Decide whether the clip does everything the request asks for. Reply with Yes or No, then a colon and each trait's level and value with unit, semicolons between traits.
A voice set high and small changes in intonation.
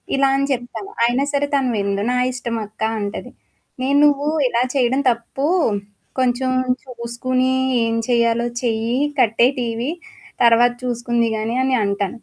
Yes: high, 240 Hz; narrow, 2.1 semitones